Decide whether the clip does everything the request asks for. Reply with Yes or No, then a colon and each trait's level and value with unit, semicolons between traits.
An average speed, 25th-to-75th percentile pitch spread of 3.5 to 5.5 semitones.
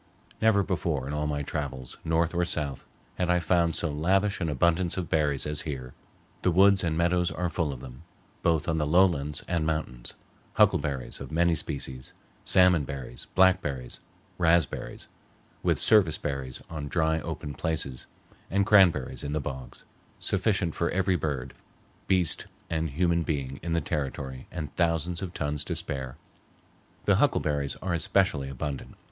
Yes: average, 155 wpm; average, 3.8 semitones